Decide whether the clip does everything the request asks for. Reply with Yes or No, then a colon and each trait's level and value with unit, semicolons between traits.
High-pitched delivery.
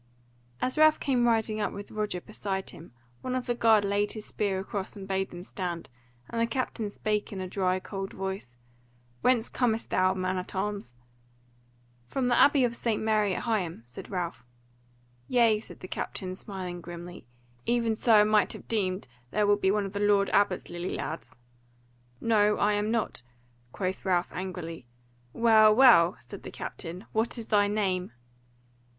Yes: high, 205 Hz